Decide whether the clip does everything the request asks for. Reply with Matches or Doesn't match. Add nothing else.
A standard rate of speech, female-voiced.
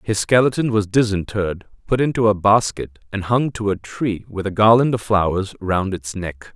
Doesn't match